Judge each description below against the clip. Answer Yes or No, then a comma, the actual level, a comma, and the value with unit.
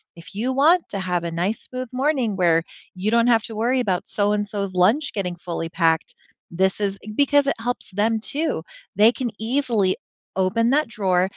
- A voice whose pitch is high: Yes, high, 210 Hz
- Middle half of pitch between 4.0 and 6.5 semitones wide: Yes, average, 5.0 semitones